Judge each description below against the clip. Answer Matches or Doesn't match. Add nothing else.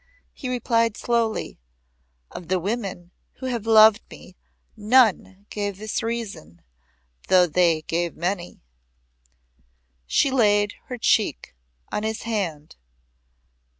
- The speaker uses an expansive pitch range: Doesn't match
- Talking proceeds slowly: Matches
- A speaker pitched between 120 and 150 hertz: Doesn't match